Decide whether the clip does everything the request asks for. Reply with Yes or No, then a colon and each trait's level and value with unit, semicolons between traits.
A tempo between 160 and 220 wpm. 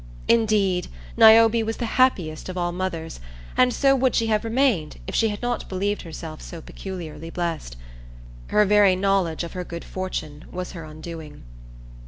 Yes: average, 165 wpm